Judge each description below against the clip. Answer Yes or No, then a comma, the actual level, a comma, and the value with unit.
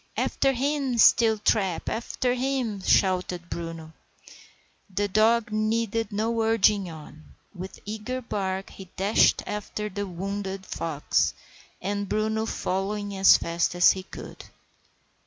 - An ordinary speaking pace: No, slow, 115 wpm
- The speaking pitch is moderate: No, high, 205 Hz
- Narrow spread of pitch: No, average, 3.0 semitones